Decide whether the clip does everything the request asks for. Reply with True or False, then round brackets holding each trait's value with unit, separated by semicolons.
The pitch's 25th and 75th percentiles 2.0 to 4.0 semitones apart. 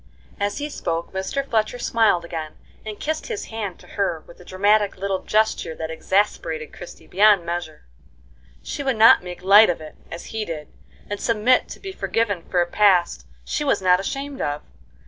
False (4.4 semitones)